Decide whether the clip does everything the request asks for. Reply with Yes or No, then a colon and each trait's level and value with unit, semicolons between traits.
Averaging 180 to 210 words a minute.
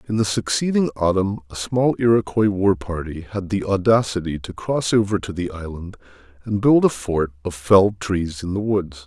Yes: average, 185 wpm